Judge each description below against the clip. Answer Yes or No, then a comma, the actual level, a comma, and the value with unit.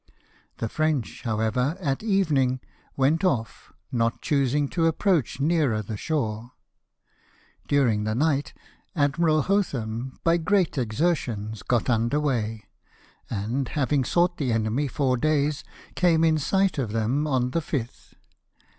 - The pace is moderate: No, slow, 130 wpm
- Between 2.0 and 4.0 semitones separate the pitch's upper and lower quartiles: No, wide, 5.4 semitones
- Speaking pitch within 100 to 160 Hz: Yes, low, 135 Hz